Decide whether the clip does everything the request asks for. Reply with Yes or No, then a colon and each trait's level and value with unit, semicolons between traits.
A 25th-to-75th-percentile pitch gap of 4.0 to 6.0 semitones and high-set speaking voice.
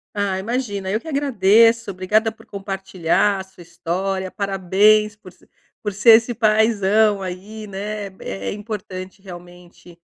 No: narrow, 2.4 semitones; high, 200 Hz